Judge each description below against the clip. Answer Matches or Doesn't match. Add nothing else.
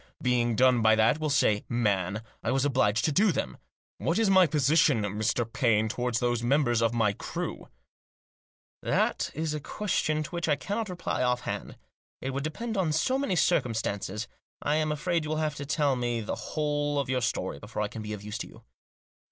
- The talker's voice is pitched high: Doesn't match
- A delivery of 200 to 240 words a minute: Matches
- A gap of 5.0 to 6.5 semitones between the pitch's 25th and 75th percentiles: Matches